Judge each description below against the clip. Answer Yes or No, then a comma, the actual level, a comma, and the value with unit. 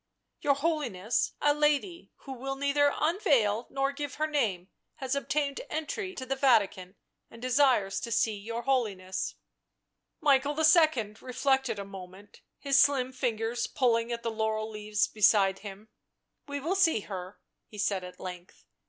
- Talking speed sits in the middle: Yes, average, 160 wpm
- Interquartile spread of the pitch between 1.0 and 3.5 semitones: No, average, 5.3 semitones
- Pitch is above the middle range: Yes, very high, 250 Hz